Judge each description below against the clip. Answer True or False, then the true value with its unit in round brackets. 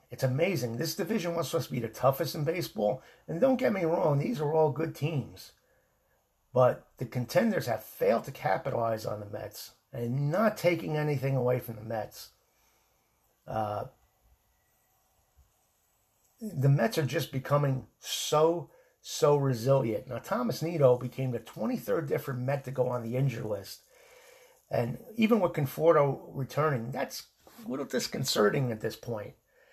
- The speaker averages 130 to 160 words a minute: True (150 wpm)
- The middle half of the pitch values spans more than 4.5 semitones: True (5.1 semitones)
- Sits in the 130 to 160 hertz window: True (140 Hz)